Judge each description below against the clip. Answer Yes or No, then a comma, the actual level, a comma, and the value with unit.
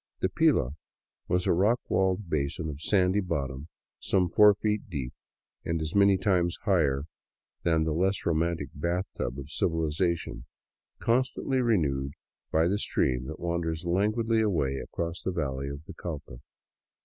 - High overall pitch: No, very low, 85 Hz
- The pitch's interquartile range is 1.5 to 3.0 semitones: No, average, 4.8 semitones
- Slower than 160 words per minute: Yes, average, 150 wpm